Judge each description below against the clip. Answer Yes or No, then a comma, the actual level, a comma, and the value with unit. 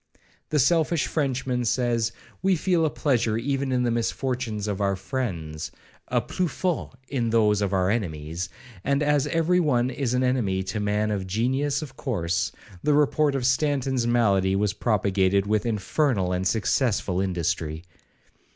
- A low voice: Yes, low, 115 Hz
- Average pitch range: No, wide, 5.8 semitones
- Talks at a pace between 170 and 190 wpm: No, average, 155 wpm